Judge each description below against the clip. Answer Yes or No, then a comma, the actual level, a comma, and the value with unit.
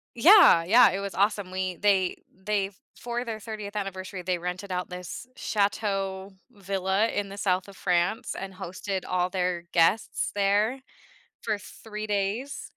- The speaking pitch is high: Yes, high, 195 Hz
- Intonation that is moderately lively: No, narrow, 2.3 semitones